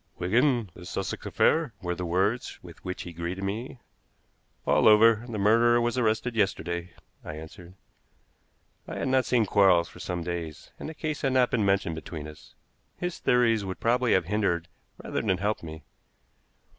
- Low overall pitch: Yes, low, 100 Hz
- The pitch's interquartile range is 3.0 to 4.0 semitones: No, wide, 5.4 semitones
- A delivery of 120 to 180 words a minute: Yes, average, 170 wpm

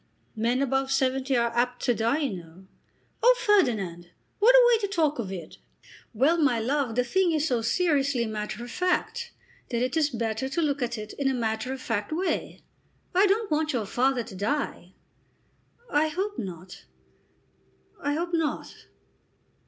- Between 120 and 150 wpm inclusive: No, average, 170 wpm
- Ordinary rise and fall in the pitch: No, wide, 5.8 semitones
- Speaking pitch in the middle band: No, very high, 265 Hz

